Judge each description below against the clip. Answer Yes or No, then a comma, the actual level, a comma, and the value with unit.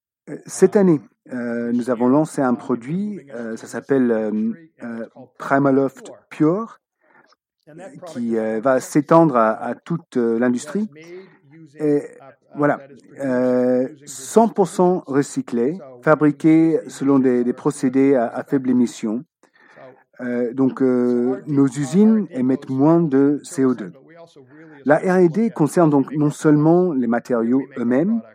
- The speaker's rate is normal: No, slow, 120 wpm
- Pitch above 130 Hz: Yes, medium, 140 Hz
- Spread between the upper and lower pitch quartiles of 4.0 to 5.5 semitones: Yes, average, 4.4 semitones